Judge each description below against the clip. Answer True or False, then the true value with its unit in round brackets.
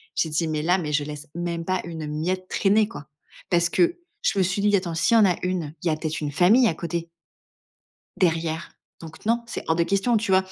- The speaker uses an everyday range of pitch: True (3.4 semitones)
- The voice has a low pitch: False (175 Hz)